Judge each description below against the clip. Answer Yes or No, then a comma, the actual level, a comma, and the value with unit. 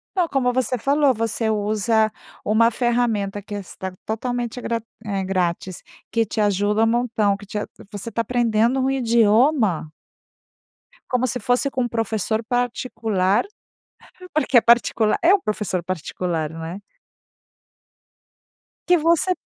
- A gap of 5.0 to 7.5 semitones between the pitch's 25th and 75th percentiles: No, average, 3.2 semitones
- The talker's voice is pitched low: No, high, 225 Hz